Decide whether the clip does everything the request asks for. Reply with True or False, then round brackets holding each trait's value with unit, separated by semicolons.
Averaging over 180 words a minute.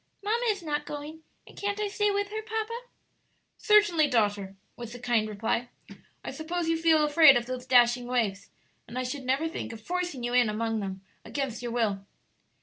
True (190 wpm)